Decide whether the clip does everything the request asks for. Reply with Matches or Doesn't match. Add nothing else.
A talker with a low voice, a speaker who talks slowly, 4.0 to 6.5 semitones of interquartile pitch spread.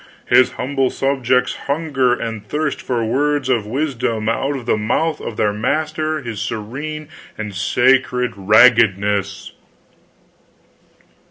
Matches